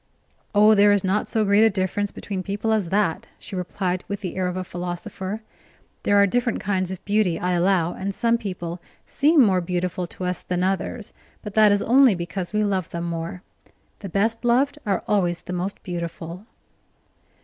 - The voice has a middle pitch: No, high, 195 Hz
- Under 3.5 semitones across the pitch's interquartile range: Yes, average, 2.7 semitones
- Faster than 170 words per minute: Yes, average, 190 wpm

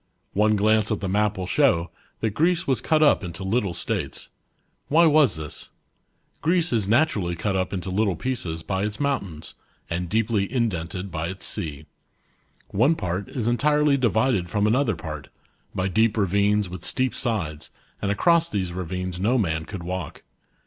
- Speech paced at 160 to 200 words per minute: Yes, average, 180 wpm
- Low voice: Yes, low, 100 Hz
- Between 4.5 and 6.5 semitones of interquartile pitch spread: Yes, average, 5.1 semitones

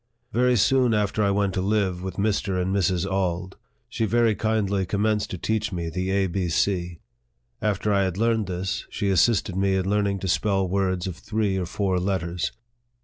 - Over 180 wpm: Yes, average, 190 wpm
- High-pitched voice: No, very low, 95 Hz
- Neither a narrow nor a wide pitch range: No, narrow, 2.2 semitones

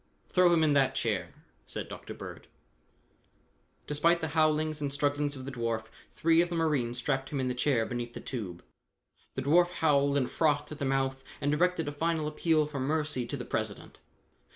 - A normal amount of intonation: Yes, average, 3.0 semitones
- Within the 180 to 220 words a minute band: Yes, average, 190 wpm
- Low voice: No, medium, 145 Hz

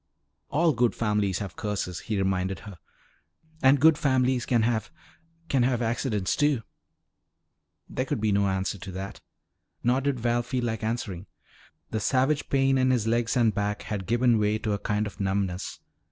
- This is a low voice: Yes, low, 115 Hz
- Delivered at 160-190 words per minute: Yes, average, 170 wpm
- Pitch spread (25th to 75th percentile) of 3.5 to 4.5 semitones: Yes, average, 4.0 semitones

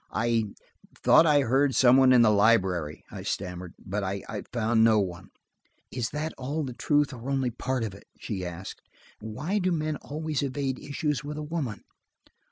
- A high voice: No, low, 125 Hz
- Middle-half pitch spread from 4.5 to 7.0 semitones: Yes, wide, 5.6 semitones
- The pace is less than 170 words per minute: No, average, 175 wpm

